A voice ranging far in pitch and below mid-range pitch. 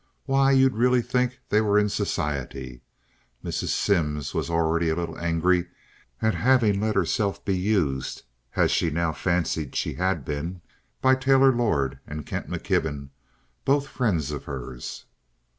Yes: wide, 7.2 semitones; very low, 90 Hz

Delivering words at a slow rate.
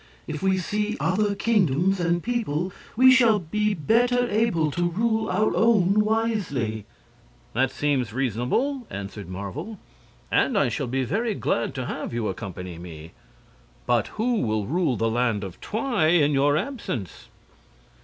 No: average, 145 wpm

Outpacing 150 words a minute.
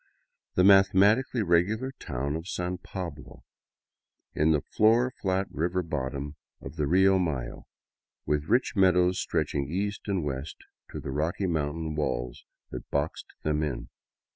No: average, 140 wpm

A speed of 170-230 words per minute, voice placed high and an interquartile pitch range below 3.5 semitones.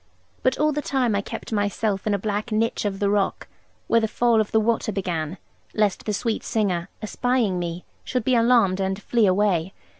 Yes: average, 200 wpm; high, 210 Hz; average, 3.0 semitones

